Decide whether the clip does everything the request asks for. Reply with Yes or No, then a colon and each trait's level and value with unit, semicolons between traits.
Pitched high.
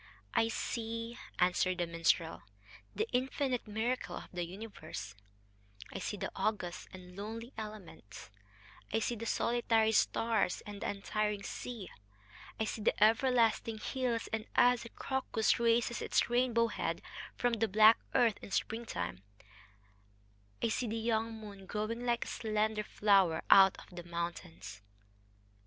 Yes: high, 220 Hz